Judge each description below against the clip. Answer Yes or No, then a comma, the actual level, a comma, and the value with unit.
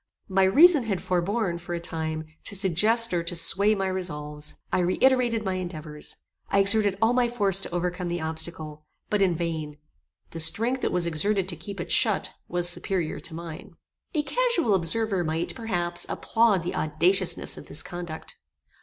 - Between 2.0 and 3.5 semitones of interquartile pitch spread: No, average, 3.9 semitones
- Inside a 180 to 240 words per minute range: No, average, 170 wpm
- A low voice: No, medium, 180 Hz